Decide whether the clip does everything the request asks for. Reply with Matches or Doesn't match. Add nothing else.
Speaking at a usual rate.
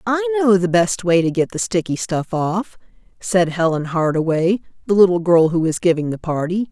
Matches